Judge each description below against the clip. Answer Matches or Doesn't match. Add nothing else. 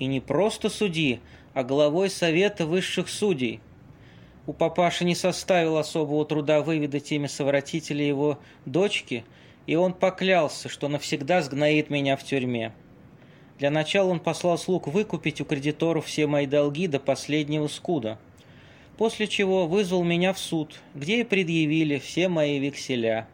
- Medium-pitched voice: Matches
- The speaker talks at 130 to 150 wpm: Matches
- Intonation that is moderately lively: Matches